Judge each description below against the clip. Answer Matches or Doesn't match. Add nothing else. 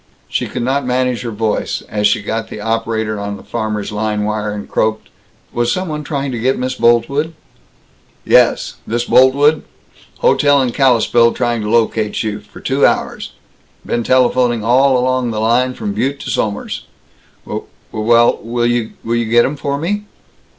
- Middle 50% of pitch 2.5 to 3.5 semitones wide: Matches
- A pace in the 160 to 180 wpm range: Matches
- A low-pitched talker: Matches